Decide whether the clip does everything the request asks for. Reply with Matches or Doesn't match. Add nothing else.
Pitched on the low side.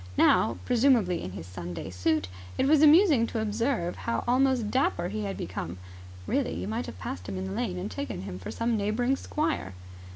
Doesn't match